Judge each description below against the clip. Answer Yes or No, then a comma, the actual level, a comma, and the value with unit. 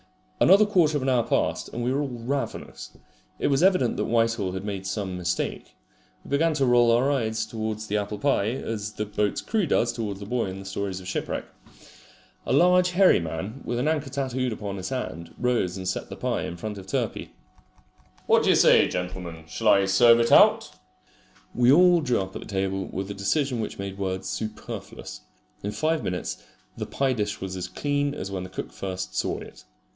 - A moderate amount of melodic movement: No, wide, 5.7 semitones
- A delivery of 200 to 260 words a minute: Yes, fast, 205 wpm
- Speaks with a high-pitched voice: No, low, 110 Hz